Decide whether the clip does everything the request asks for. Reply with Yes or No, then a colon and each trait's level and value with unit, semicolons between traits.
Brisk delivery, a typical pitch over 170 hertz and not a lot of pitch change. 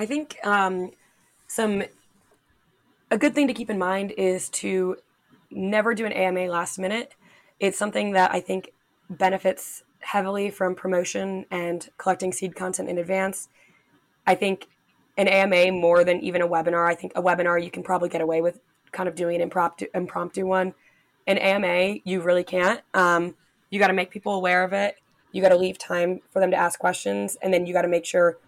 No: average, 190 wpm; medium, 185 Hz; narrow, 1.7 semitones